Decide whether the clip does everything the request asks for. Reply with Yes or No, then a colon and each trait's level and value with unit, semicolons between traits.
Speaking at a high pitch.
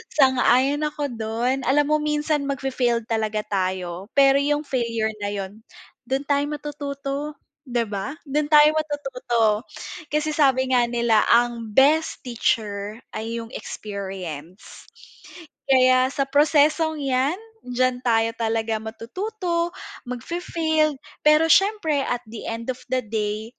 Yes: very high, 255 Hz